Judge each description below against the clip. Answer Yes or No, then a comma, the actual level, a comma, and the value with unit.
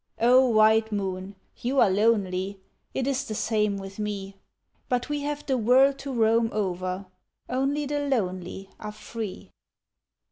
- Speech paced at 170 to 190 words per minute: No, average, 145 wpm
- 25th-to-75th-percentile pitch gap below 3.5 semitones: No, average, 4.9 semitones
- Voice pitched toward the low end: No, high, 220 Hz